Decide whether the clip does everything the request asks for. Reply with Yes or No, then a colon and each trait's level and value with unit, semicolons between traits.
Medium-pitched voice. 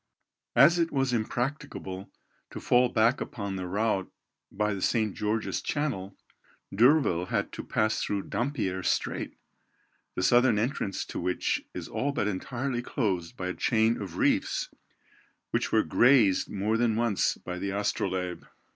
No: low, 110 Hz